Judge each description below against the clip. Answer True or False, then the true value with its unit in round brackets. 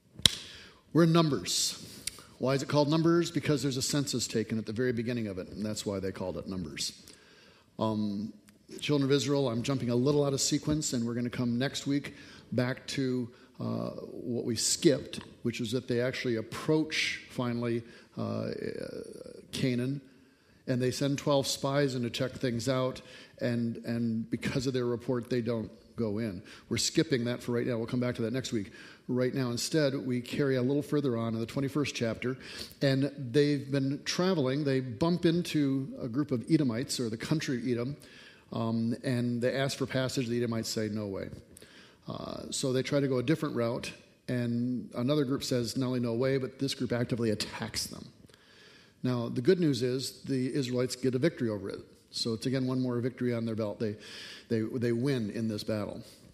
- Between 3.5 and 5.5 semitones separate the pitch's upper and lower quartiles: False (2.8 semitones)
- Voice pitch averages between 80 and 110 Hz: False (125 Hz)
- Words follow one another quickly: False (195 wpm)